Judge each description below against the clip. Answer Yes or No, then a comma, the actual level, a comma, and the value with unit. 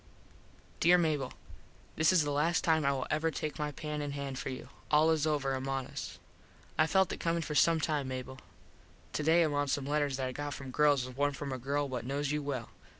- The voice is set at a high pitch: No, medium, 145 Hz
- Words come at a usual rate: No, fast, 225 wpm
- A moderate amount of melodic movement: No, narrow, 2.3 semitones